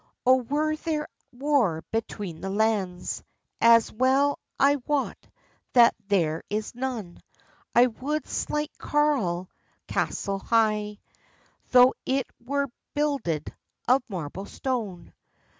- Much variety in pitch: Yes, wide, 5.9 semitones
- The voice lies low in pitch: No, high, 235 Hz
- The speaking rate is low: Yes, slow, 110 wpm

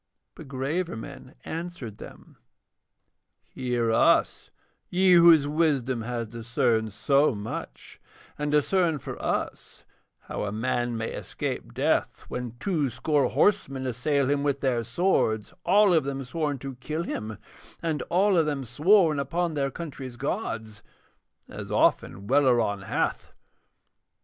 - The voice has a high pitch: No, low, 135 Hz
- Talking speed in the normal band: No, slow, 130 wpm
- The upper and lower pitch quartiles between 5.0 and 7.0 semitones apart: Yes, average, 5.3 semitones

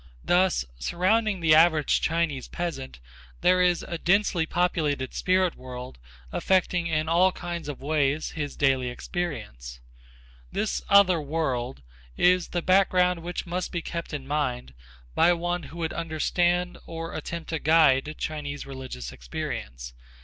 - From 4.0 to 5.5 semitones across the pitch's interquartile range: Yes, average, 4.3 semitones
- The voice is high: No, medium, 165 Hz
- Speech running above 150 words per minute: No, slow, 135 wpm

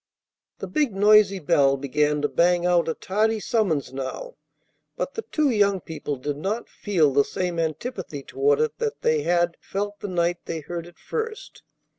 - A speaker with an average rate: Yes, average, 175 wpm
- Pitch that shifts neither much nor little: No, wide, 6.2 semitones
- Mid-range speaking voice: Yes, medium, 180 Hz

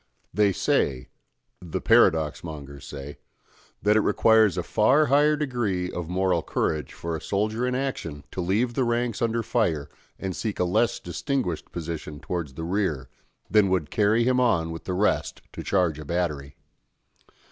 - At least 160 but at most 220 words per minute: Yes, average, 165 wpm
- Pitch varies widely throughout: Yes, wide, 5.8 semitones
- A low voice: Yes, very low, 95 Hz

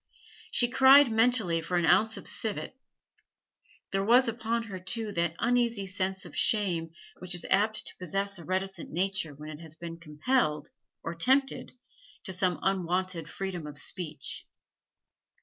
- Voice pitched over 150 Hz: Yes, high, 190 Hz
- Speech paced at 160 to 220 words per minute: No, average, 150 wpm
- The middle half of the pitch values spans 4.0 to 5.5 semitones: Yes, average, 4.7 semitones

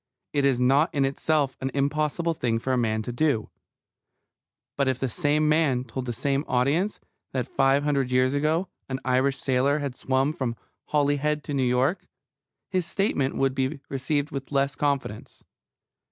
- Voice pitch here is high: No, medium, 140 Hz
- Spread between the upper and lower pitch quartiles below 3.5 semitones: Yes, narrow, 2.5 semitones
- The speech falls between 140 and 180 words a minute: Yes, average, 170 wpm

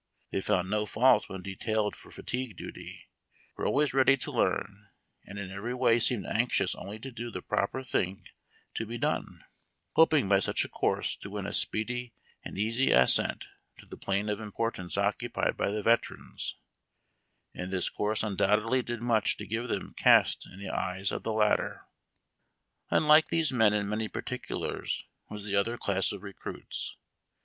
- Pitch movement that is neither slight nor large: Yes, average, 3.2 semitones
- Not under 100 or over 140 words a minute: No, average, 170 wpm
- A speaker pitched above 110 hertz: No, low, 105 Hz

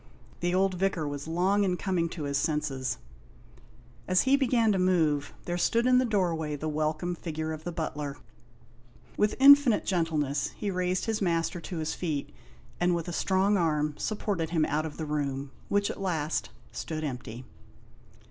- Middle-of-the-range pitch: Yes, medium, 170 Hz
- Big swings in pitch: No, average, 4.0 semitones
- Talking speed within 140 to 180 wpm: Yes, average, 170 wpm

